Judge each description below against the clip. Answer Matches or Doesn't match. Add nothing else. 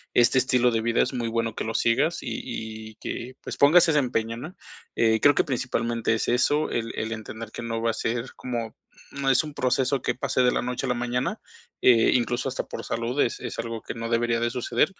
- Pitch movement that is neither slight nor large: Doesn't match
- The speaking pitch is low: Matches